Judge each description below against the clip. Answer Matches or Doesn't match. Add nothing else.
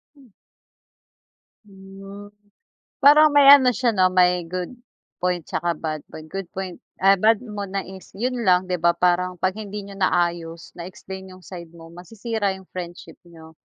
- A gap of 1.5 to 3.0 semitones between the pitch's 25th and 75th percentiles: Matches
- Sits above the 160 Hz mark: Matches